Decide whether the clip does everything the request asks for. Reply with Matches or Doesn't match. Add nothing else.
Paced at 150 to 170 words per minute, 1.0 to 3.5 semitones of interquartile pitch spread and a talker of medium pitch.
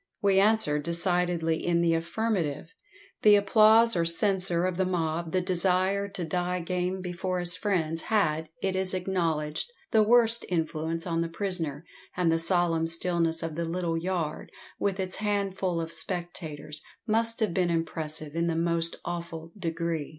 Matches